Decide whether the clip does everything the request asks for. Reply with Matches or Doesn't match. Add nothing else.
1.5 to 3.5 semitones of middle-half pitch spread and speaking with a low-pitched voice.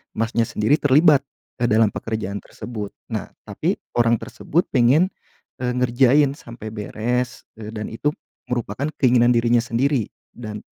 Matches